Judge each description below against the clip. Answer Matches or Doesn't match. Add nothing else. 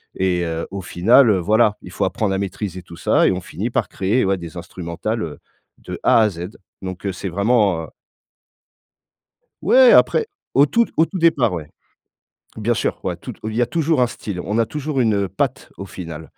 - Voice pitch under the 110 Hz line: Matches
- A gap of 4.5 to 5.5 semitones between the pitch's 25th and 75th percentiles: Matches